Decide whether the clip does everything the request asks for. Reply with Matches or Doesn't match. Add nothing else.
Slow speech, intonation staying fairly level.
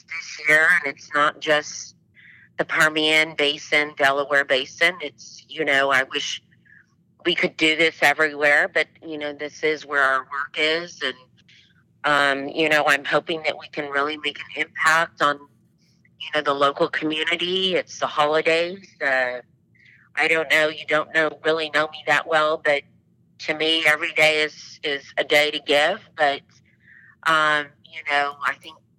Doesn't match